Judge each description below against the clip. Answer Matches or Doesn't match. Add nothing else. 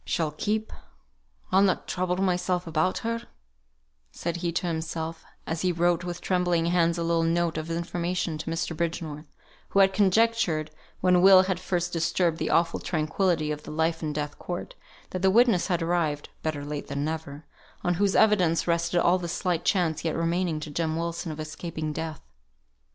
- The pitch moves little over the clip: Matches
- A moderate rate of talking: Matches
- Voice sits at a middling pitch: Matches